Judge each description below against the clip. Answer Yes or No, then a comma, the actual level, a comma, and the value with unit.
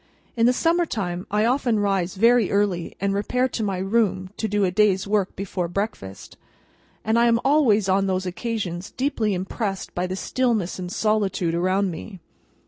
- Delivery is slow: No, average, 175 wpm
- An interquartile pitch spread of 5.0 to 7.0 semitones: No, average, 3.4 semitones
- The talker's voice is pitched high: Yes, high, 200 Hz